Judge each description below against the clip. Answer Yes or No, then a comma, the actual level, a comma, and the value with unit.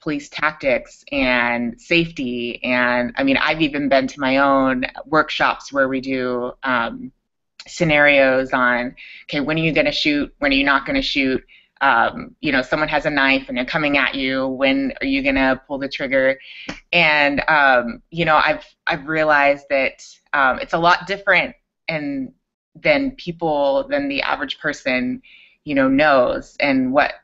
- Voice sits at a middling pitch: Yes, medium, 150 Hz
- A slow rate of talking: No, average, 165 wpm